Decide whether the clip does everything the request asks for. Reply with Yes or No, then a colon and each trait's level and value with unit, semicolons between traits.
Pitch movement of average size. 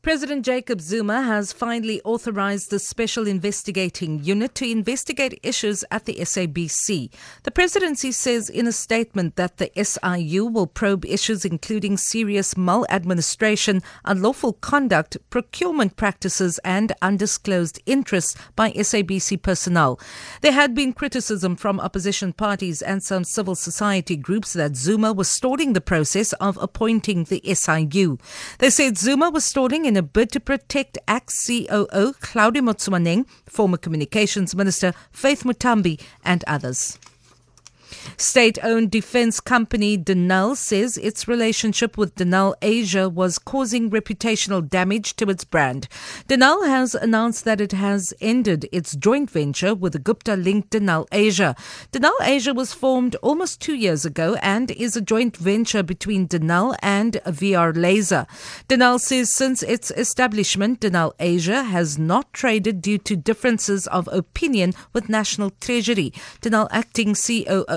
Yes: average, 4.0 semitones